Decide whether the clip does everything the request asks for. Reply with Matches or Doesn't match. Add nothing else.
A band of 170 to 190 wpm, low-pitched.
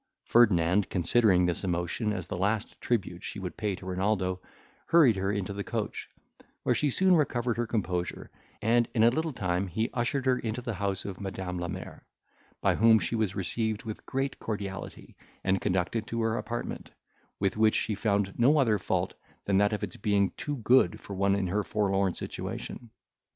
Matches